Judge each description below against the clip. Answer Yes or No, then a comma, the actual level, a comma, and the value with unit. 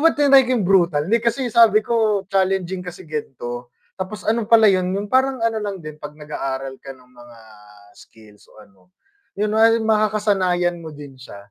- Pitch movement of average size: No, wide, 6.8 semitones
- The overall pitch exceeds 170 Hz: Yes, high, 190 Hz